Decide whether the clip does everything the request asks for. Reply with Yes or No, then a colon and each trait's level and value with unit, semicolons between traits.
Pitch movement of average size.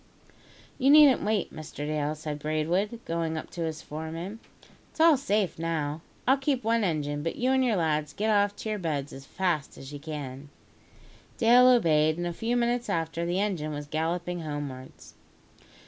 No: wide, 6.1 semitones